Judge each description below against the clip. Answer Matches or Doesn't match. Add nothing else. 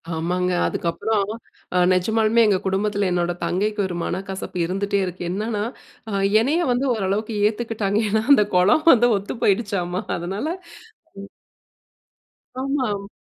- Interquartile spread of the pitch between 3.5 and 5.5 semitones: Doesn't match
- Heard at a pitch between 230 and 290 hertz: Doesn't match